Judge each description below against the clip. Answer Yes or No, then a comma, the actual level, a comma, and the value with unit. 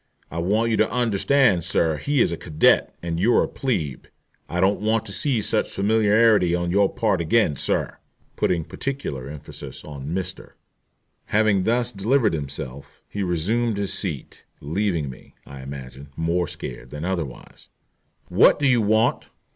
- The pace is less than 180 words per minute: Yes, average, 160 wpm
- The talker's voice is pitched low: Yes, very low, 95 Hz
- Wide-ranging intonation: Yes, wide, 5.7 semitones